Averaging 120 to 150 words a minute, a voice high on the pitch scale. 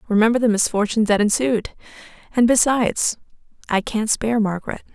Yes: slow, 135 wpm; high, 220 Hz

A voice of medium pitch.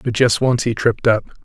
No: low, 120 Hz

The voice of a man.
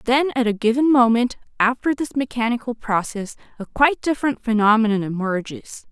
No: female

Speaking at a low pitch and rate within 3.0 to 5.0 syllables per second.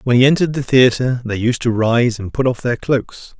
No: low, 125 Hz; 5.2 syllables/s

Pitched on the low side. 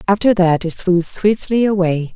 No: high, 190 Hz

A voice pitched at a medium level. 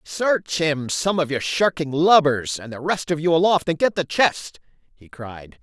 Yes: medium, 155 Hz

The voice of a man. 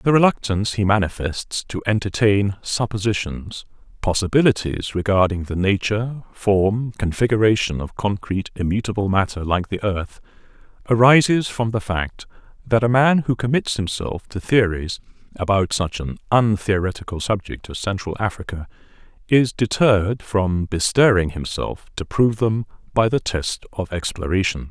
Yes: male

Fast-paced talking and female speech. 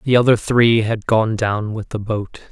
No: fast, 215 wpm; male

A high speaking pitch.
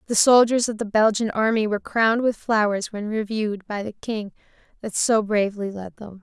Yes: high, 215 Hz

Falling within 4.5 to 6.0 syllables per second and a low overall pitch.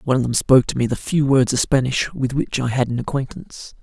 No: 6.2 syllables/s; low, 130 Hz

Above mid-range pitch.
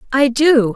Yes: very high, 260 Hz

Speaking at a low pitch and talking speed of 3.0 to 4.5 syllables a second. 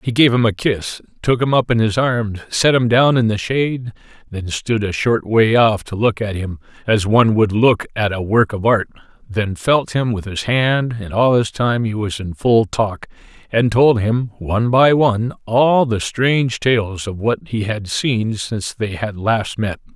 Yes: low, 110 Hz; 4.4 syllables/s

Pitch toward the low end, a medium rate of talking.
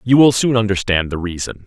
No: low, 105 Hz; fast, 215 wpm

